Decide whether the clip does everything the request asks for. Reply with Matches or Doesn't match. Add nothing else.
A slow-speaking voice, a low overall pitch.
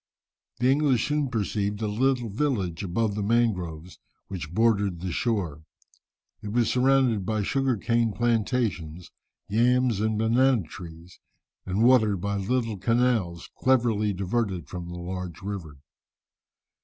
Matches